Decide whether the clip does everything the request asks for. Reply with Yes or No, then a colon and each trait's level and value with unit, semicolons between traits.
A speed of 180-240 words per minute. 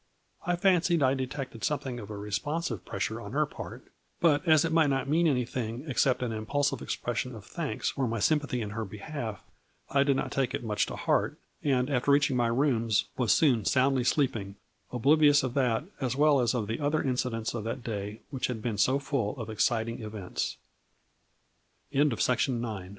No: average, 155 wpm